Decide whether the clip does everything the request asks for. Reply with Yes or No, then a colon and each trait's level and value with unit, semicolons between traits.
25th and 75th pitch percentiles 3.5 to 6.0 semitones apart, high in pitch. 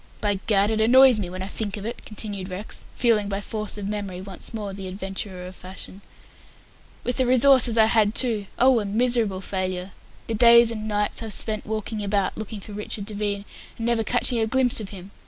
No: narrow, 2.5 semitones; high, 210 Hz